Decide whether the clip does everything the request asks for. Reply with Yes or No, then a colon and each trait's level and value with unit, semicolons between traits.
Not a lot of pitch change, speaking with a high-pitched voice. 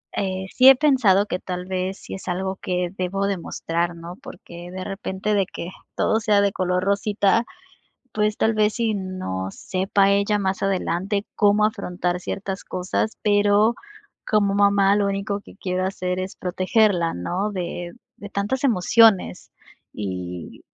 Yes: narrow, 2.1 semitones; high, 195 Hz